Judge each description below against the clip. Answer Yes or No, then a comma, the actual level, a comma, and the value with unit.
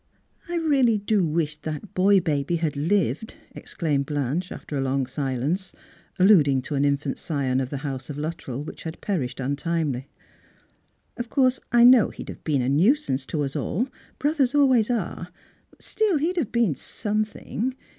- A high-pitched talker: No, medium, 165 Hz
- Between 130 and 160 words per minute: No, average, 180 wpm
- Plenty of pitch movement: Yes, wide, 8.0 semitones